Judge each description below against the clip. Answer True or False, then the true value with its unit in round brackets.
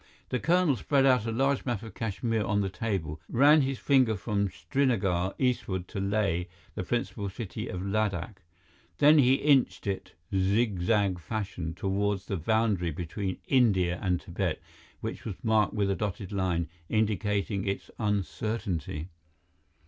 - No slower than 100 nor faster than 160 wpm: True (145 wpm)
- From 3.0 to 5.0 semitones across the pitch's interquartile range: True (3.6 semitones)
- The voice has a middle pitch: False (100 Hz)